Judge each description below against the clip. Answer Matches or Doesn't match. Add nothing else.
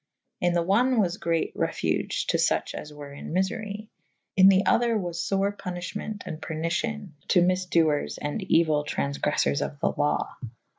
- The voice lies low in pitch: Doesn't match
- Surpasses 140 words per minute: Matches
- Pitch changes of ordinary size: Matches